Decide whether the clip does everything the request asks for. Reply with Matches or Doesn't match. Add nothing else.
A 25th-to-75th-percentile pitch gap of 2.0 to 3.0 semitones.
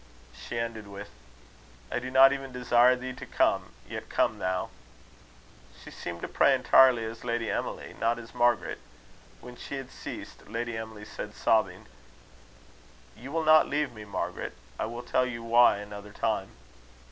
Matches